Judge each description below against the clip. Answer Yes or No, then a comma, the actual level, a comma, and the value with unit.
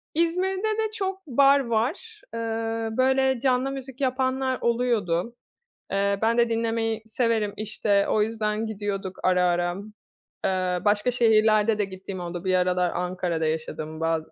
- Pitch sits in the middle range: No, high, 225 Hz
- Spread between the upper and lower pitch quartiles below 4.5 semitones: No, wide, 5.4 semitones